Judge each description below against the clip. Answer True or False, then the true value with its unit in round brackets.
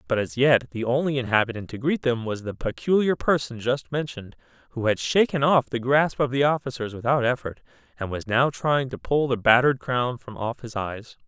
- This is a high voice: False (125 Hz)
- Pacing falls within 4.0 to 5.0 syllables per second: False (5.4 syllables/s)